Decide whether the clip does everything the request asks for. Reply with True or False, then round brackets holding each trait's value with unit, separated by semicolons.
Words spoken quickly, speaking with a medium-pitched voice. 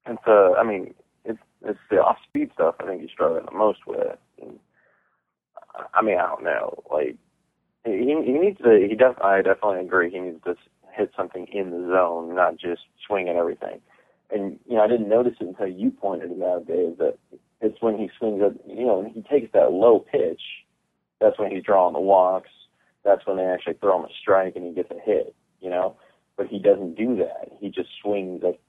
False (215 wpm; 110 Hz)